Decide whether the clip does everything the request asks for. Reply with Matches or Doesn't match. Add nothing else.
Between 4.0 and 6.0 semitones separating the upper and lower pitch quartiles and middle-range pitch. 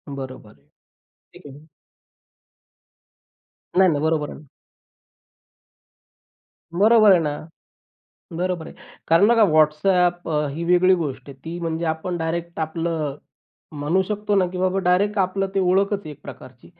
Doesn't match